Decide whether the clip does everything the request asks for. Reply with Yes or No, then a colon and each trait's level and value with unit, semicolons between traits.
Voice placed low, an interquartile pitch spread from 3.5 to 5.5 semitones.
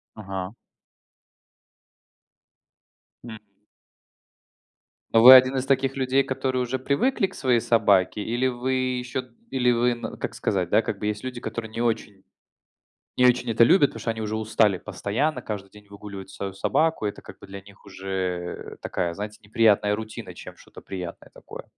Yes: low, 115 Hz; average, 4.1 semitones